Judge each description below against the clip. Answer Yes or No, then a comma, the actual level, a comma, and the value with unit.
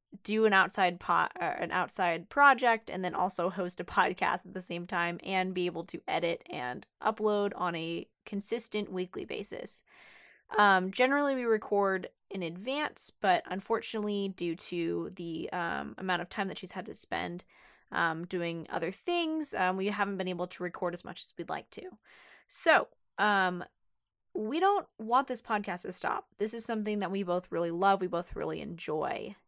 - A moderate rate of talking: Yes, average, 180 wpm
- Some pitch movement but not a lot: Yes, average, 3.6 semitones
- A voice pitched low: No, high, 190 Hz